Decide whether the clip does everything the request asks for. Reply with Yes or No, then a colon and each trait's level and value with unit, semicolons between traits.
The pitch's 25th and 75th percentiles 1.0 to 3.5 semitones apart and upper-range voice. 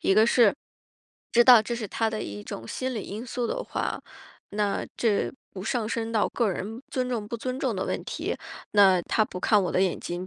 Yes: average, 3.2 semitones; high, 220 Hz